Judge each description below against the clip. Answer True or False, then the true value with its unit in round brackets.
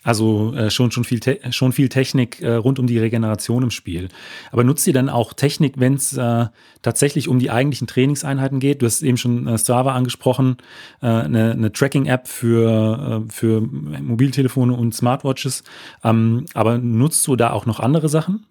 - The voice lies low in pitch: True (125 Hz)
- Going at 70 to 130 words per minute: False (185 wpm)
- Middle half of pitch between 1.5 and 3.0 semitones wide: True (2.7 semitones)